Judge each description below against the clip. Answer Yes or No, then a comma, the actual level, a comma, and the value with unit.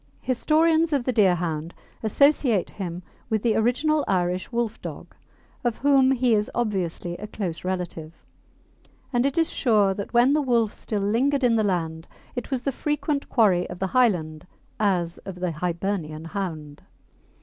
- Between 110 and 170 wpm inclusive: Yes, average, 155 wpm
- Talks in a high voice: Yes, high, 210 Hz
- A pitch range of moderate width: No, wide, 6.1 semitones